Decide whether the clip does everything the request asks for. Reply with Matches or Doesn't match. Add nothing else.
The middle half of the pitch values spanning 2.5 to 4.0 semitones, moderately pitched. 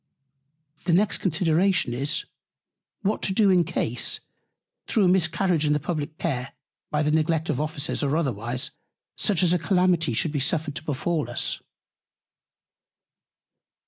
Matches